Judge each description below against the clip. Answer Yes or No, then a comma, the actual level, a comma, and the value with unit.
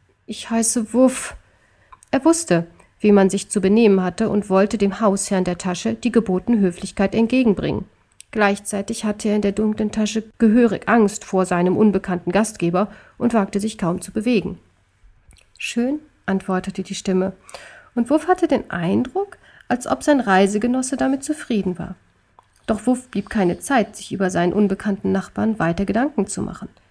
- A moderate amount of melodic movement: Yes, average, 3.2 semitones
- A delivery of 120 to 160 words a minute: Yes, average, 155 wpm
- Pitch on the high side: Yes, high, 205 Hz